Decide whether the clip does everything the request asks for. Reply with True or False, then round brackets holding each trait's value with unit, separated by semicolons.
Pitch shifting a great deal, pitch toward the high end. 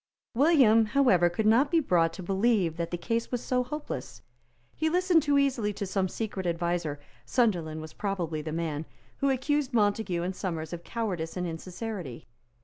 True (6.5 semitones; 195 Hz)